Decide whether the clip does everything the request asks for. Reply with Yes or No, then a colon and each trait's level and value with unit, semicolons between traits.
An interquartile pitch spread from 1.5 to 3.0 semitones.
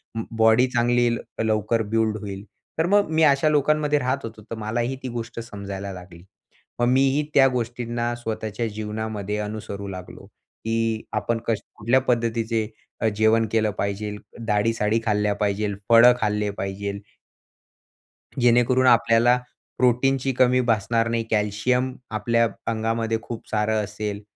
Yes: narrow, 2.5 semitones